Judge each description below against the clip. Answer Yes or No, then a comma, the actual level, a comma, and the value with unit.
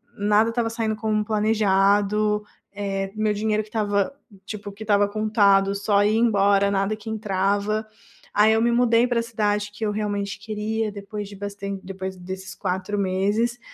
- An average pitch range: No, narrow, 1.4 semitones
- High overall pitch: Yes, high, 210 Hz